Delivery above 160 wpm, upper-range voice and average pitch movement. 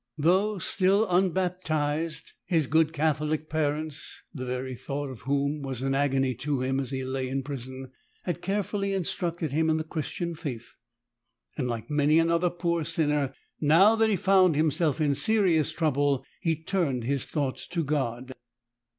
No: average, 170 wpm; medium, 155 Hz; average, 3.9 semitones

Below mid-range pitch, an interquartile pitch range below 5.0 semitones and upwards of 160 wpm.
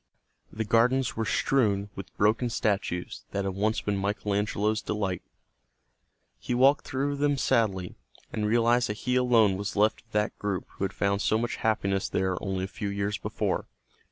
Yes: low, 105 Hz; average, 2.8 semitones; average, 175 wpm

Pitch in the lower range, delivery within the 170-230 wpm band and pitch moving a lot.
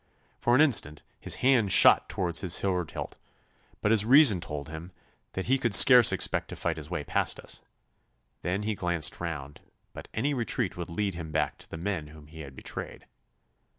Yes: very low, 90 Hz; average, 190 wpm; wide, 5.7 semitones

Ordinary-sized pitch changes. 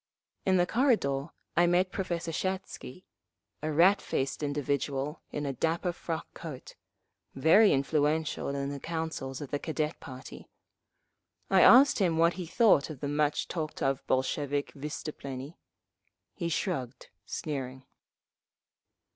Yes: average, 3.7 semitones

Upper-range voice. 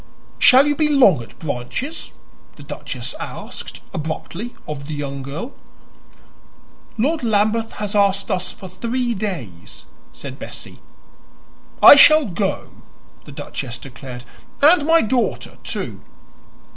Yes: high, 200 Hz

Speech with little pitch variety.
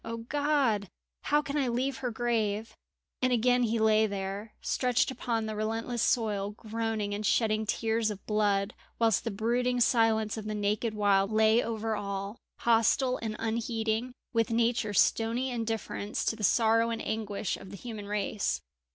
Yes: narrow, 1.9 semitones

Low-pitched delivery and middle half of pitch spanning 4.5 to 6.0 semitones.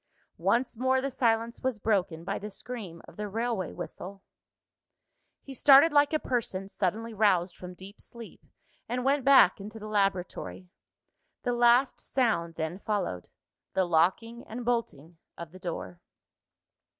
No: high, 215 Hz; average, 5.0 semitones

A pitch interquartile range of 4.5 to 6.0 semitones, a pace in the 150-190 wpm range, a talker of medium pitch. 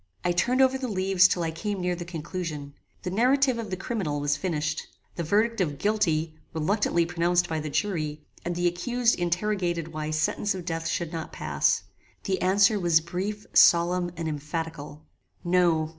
No: average, 3.7 semitones; average, 175 wpm; medium, 175 Hz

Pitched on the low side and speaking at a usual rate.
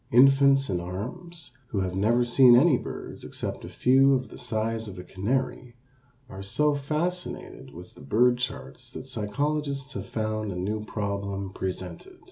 Yes: low, 120 Hz; average, 160 wpm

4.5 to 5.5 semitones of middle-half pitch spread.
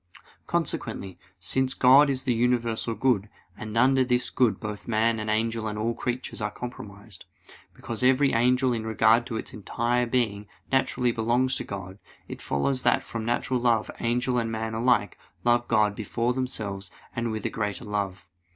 No: narrow, 2.5 semitones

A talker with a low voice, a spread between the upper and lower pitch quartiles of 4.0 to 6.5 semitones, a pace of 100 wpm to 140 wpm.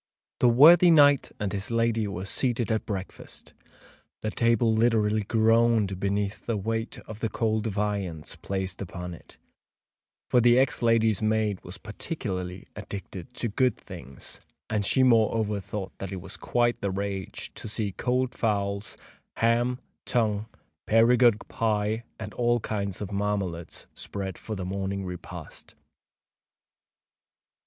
No: low, 105 Hz; average, 3.0 semitones; slow, 135 wpm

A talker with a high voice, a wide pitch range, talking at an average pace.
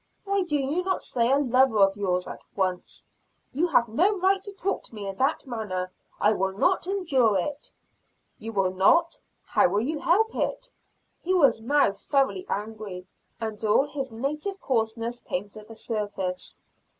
Yes: high, 240 Hz; wide, 7.6 semitones; average, 175 wpm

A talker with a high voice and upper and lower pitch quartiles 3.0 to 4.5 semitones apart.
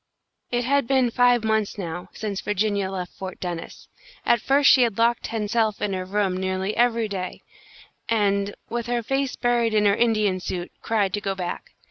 Yes: high, 210 Hz; average, 3.6 semitones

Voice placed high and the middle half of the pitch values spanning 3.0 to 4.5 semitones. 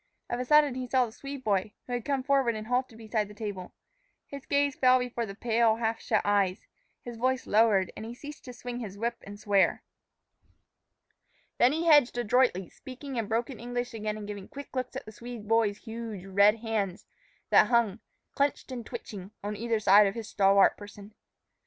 Yes: high, 230 Hz; average, 3.3 semitones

